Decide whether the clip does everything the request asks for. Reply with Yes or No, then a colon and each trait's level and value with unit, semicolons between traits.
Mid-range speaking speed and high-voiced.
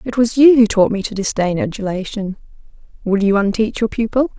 Yes: average, 190 wpm; high, 215 Hz